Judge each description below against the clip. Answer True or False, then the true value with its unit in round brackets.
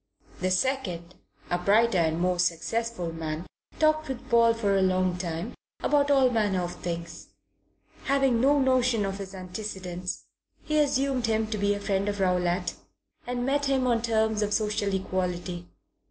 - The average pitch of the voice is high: True (205 Hz)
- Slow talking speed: False (160 wpm)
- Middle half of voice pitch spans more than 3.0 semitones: True (5.2 semitones)